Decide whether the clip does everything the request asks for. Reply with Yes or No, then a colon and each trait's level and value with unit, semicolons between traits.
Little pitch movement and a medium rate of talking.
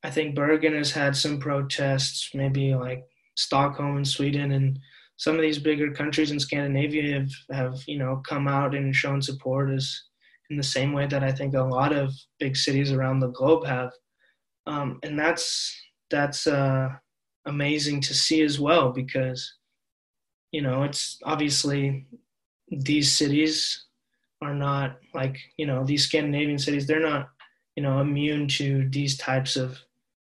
Yes: narrow, 1.6 semitones; average, 160 wpm